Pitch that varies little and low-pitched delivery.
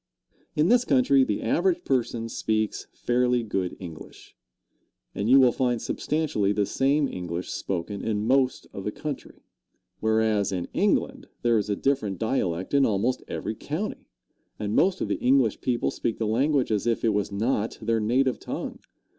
No: average, 4.5 semitones; low, 115 Hz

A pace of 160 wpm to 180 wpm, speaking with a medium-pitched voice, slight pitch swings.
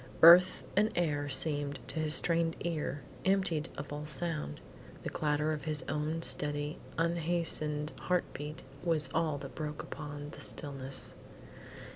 No: average, 140 wpm; medium, 150 Hz; narrow, 2.2 semitones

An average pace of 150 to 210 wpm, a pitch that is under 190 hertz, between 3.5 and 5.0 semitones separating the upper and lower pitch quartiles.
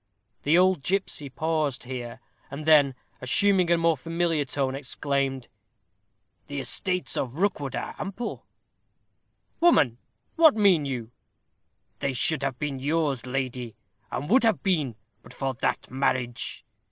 No: slow, 135 wpm; medium, 140 Hz; average, 4.5 semitones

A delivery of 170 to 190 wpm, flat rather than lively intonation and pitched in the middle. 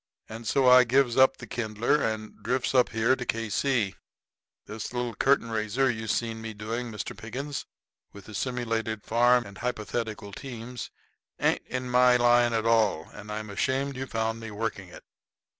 No: average, 175 wpm; narrow, 2.3 semitones; low, 115 Hz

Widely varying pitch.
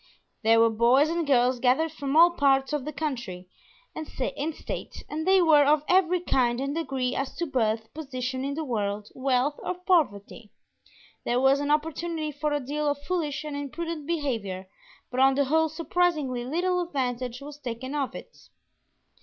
No: average, 4.0 semitones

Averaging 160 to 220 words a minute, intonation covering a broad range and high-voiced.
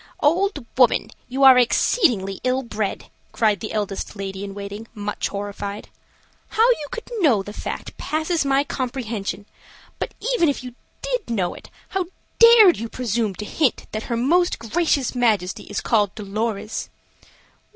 No: average, 150 wpm; wide, 6.0 semitones; high, 235 Hz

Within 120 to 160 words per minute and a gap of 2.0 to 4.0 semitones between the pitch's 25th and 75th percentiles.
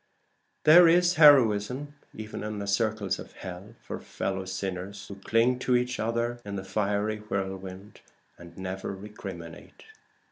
Yes: average, 140 wpm; average, 3.6 semitones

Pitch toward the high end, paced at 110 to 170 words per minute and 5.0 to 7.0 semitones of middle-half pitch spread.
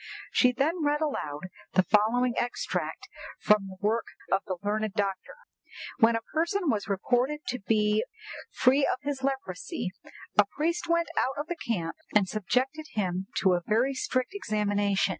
Yes: high, 230 Hz; average, 160 wpm; wide, 5.5 semitones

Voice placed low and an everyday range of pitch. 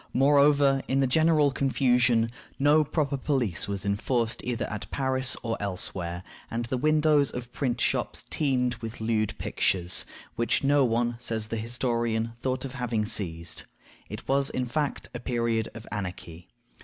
Yes: low, 120 Hz; average, 3.4 semitones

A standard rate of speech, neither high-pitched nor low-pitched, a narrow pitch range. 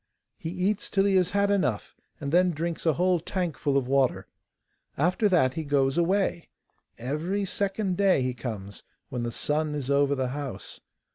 No: average, 170 wpm; medium, 160 Hz; wide, 5.4 semitones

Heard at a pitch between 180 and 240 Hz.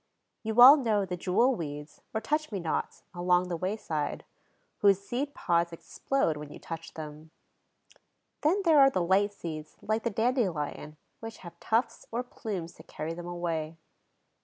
Yes: medium, 185 Hz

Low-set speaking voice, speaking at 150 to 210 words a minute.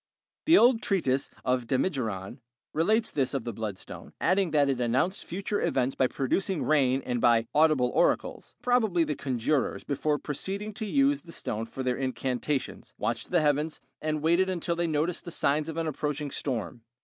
No: medium, 150 Hz; average, 175 wpm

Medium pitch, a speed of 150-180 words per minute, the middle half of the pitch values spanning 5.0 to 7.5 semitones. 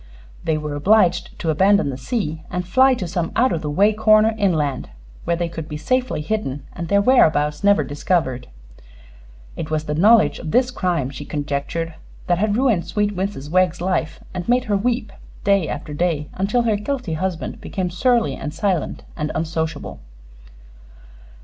Yes: medium, 180 Hz; average, 170 wpm; average, 5.3 semitones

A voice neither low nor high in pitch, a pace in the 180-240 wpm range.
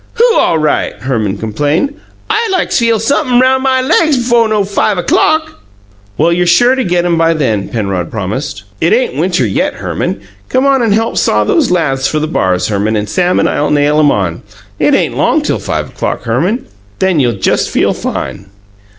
Yes: medium, 170 Hz; average, 195 wpm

